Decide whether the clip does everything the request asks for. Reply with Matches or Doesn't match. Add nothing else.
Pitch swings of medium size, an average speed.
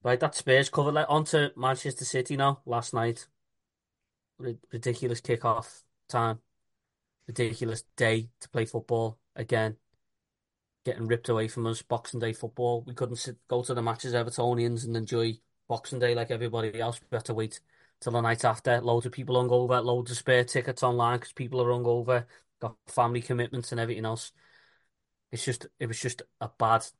Doesn't match